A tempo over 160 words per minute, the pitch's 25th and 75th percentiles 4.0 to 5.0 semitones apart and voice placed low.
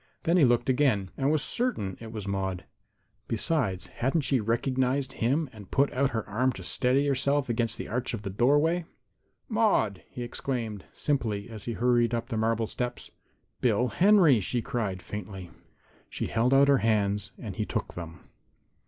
Yes: average, 170 wpm; average, 4.6 semitones; low, 120 Hz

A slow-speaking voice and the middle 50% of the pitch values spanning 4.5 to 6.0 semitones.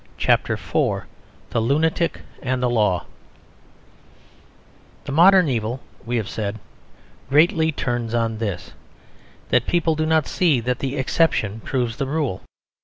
Yes: slow, 130 wpm; wide, 5.6 semitones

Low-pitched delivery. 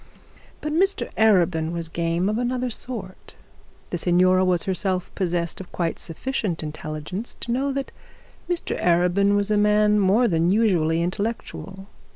No: high, 190 Hz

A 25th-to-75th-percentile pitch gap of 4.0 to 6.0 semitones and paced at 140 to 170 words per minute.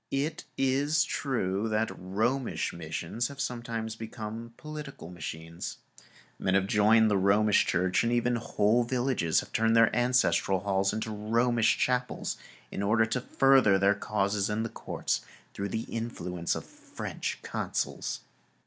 No: average, 3.6 semitones; average, 145 wpm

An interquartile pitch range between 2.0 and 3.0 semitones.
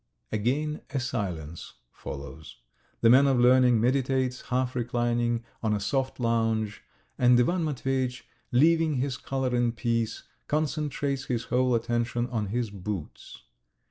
Yes: narrow, 2.5 semitones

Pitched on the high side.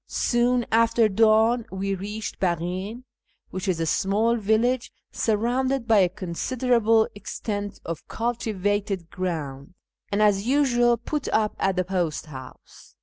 Yes: high, 210 Hz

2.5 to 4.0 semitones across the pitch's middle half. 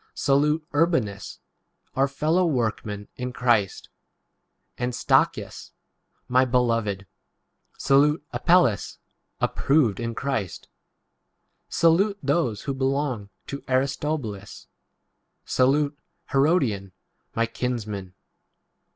No: average, 4.7 semitones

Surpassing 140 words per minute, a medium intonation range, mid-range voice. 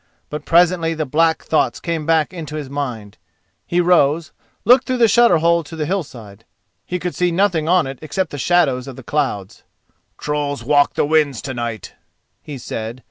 Yes: average, 185 wpm; average, 4.2 semitones; medium, 155 Hz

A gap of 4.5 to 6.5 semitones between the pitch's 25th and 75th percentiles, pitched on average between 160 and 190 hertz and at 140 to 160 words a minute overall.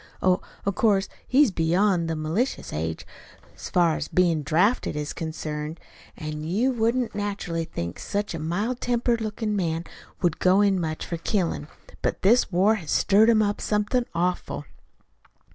Yes: average, 4.8 semitones; medium, 185 Hz; average, 155 wpm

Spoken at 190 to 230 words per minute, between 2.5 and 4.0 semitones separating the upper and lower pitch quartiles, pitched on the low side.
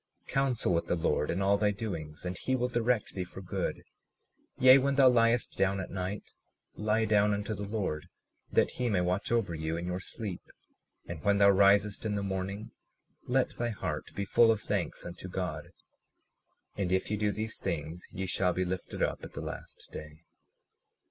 Yes: average, 195 wpm; average, 3.4 semitones; low, 100 Hz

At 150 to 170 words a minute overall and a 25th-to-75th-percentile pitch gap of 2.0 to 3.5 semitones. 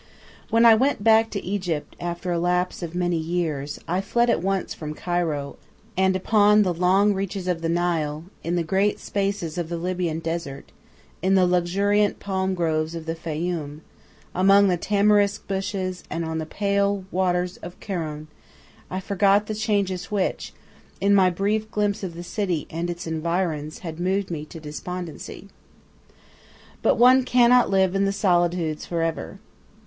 Yes: average, 165 wpm; average, 3.1 semitones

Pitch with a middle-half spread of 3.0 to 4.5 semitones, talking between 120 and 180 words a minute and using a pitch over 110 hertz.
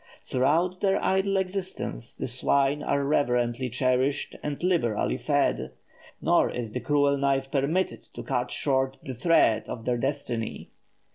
Yes: average, 4.2 semitones; average, 140 wpm; medium, 140 Hz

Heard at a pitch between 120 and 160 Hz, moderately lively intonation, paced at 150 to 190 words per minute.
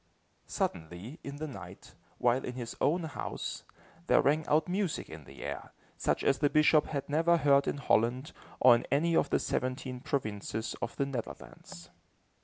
Yes: medium, 140 Hz; average, 4.4 semitones; average, 170 wpm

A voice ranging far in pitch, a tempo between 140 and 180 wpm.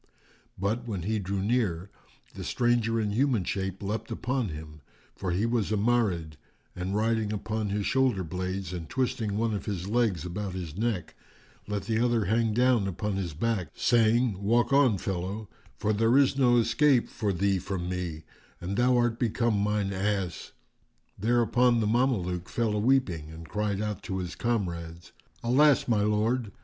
No: average, 4.0 semitones; average, 165 wpm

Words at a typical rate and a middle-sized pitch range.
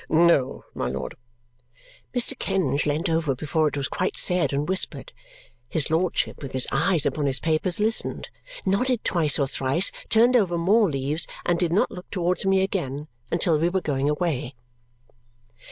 Yes: average, 165 wpm; average, 4.5 semitones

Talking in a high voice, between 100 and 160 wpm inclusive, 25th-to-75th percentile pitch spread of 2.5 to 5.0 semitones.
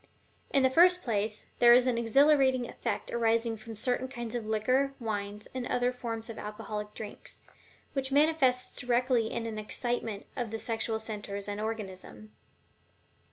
Yes: high, 230 Hz; average, 155 wpm; average, 2.8 semitones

